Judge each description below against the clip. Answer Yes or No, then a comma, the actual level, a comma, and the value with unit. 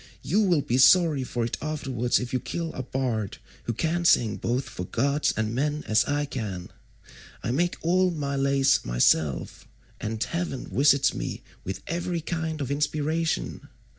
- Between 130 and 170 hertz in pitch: Yes, medium, 140 Hz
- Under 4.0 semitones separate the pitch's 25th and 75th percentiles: No, average, 5.3 semitones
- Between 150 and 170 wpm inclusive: Yes, average, 165 wpm